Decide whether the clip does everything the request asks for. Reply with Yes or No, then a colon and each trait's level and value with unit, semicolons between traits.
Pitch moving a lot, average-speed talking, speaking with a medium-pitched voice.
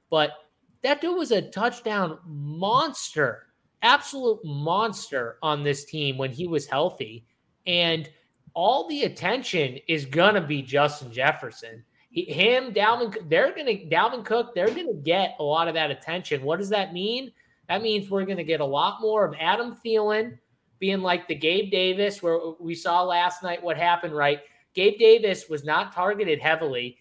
Yes: wide, 6.4 semitones; average, 170 wpm; medium, 175 Hz